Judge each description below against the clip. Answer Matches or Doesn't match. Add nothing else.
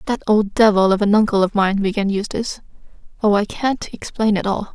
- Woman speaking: Matches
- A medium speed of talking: Matches